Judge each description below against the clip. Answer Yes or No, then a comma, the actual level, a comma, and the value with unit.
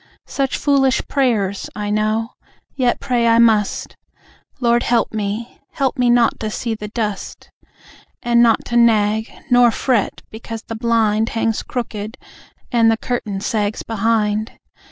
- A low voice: No, high, 225 Hz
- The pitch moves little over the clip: Yes, narrow, 2.0 semitones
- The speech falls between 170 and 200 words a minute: No, average, 145 wpm